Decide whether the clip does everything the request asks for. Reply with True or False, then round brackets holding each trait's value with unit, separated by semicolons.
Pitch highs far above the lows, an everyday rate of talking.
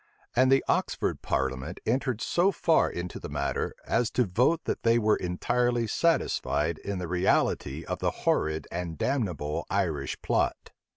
True (6.6 semitones; 155 wpm)